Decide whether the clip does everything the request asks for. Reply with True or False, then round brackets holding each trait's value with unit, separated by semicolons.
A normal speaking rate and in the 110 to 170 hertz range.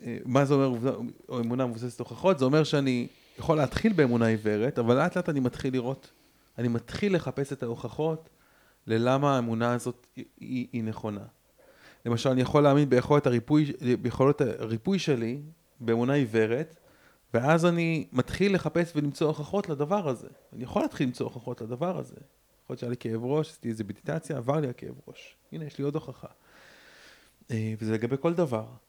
False (165 wpm; 135 Hz)